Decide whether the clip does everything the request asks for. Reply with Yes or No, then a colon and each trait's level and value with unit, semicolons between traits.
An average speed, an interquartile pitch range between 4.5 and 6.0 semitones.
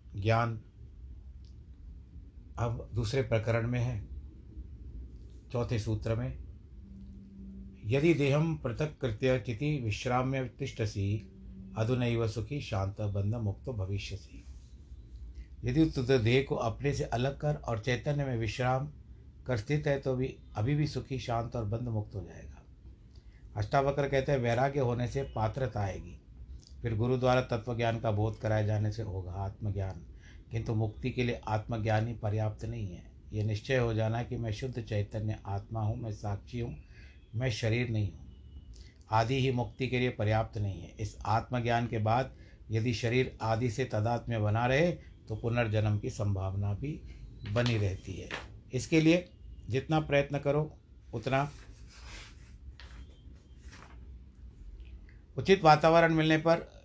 Yes: average, 140 wpm; average, 4.8 semitones